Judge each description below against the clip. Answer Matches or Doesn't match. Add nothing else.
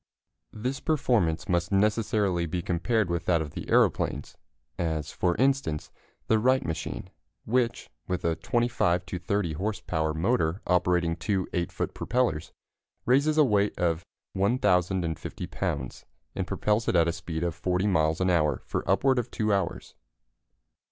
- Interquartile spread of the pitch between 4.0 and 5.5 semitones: Matches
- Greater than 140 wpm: Matches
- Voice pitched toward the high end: Doesn't match